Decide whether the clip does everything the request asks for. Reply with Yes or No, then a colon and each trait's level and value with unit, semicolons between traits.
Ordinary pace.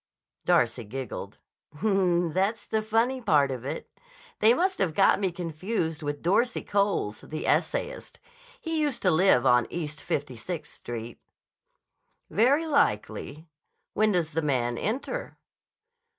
No: slow, 130 wpm